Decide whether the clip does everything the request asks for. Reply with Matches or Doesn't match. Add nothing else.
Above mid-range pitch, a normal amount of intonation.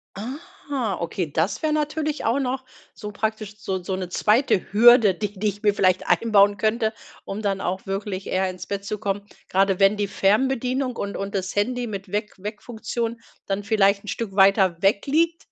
Matches